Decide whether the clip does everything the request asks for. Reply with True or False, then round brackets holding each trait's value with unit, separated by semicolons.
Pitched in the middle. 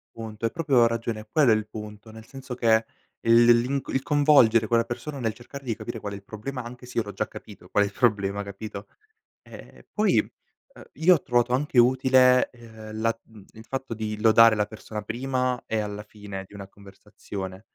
False (115 Hz)